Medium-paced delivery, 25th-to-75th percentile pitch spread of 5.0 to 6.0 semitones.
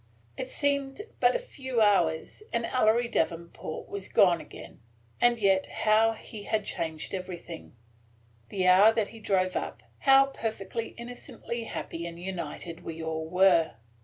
Yes: average, 145 wpm; wide, 5.4 semitones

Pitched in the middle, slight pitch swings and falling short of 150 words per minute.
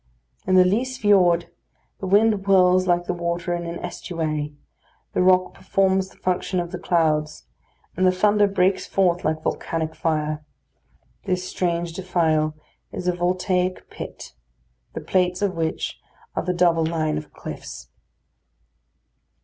Yes: medium, 180 Hz; narrow, 2.1 semitones; average, 140 wpm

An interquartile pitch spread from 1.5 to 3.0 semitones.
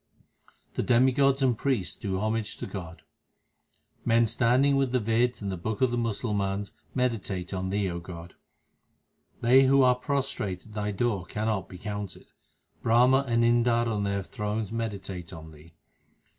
No: average, 4.0 semitones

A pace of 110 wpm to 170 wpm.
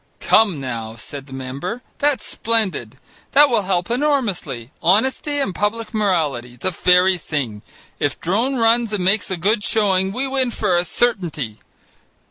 Yes: average, 150 wpm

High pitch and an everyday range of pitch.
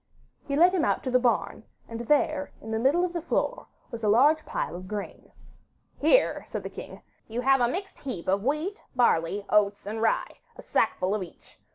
No: high, 245 Hz; wide, 6.4 semitones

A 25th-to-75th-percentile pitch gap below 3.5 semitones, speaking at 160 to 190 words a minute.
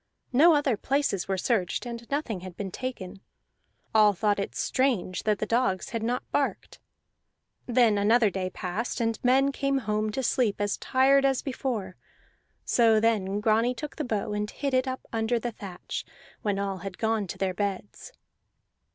No: average, 4.2 semitones; average, 170 wpm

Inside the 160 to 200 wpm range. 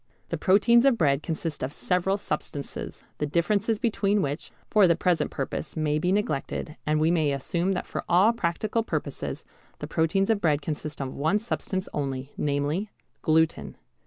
Yes: average, 165 wpm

